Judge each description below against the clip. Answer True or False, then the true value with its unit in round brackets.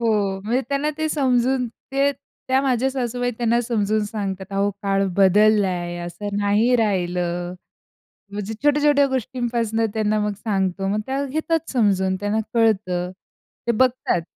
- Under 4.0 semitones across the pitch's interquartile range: False (4.3 semitones)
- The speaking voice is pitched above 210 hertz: True (220 Hz)